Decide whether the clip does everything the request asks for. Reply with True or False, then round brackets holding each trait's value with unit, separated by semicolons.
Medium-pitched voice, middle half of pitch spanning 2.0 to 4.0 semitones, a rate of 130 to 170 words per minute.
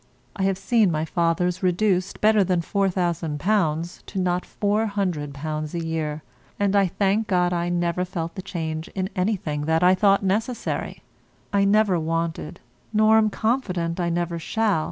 True (180 Hz; 3.3 semitones; 155 wpm)